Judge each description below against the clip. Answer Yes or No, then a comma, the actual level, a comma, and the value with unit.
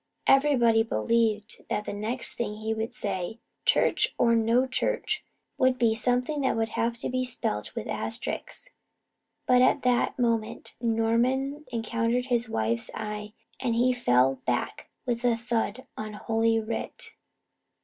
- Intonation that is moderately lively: No, narrow, 2.3 semitones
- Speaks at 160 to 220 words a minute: No, average, 145 wpm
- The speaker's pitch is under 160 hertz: No, high, 230 Hz